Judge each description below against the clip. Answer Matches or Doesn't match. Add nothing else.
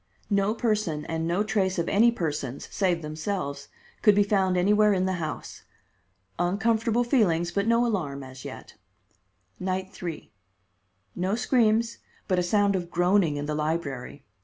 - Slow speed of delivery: Doesn't match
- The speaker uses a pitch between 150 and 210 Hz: Matches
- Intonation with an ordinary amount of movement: Matches